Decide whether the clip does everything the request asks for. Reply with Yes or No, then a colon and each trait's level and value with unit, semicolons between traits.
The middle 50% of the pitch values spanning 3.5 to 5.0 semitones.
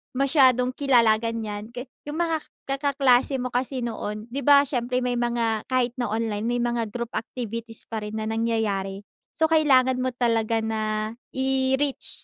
No: average, 2.9 semitones